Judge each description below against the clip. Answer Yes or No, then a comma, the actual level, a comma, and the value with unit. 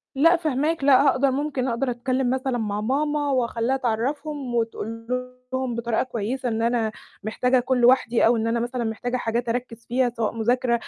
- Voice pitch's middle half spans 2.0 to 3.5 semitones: Yes, narrow, 2.4 semitones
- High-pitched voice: Yes, high, 245 Hz